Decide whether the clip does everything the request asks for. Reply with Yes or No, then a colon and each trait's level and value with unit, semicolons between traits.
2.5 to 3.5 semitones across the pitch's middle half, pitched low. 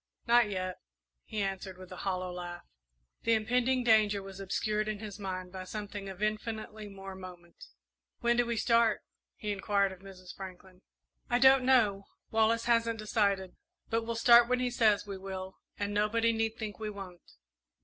No: average, 3.0 semitones; high, 210 Hz